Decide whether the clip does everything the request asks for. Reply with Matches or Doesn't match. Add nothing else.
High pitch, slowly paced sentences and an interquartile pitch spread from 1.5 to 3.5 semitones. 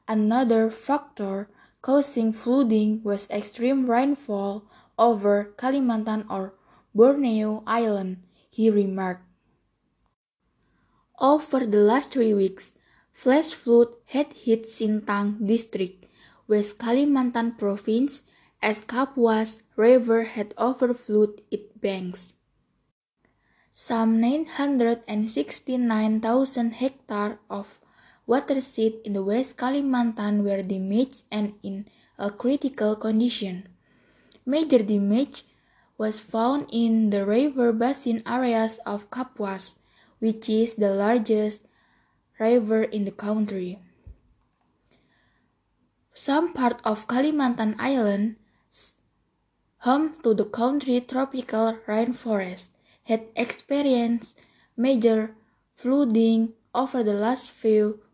Matches